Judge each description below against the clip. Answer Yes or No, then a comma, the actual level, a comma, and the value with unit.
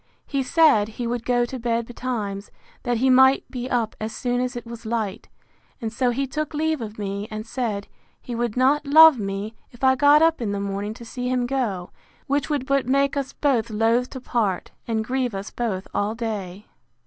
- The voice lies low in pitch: No, high, 240 Hz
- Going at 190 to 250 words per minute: Yes, fast, 205 wpm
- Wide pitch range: No, average, 3.4 semitones